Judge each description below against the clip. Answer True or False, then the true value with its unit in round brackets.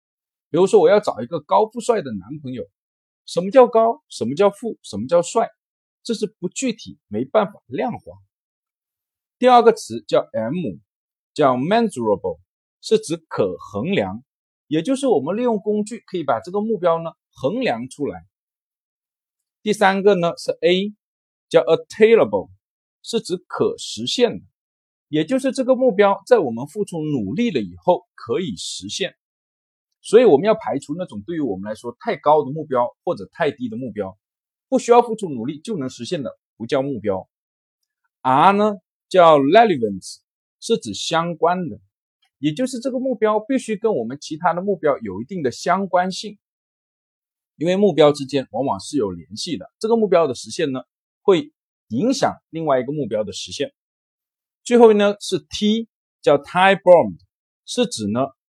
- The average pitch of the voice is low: False (200 Hz)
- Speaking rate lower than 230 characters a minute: False (265 characters per minute)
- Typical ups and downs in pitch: False (7.4 semitones)